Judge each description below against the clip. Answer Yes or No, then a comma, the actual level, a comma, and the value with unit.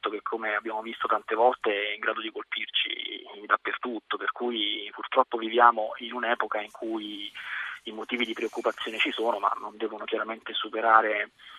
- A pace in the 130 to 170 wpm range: Yes, average, 160 wpm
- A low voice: Yes, low, 120 Hz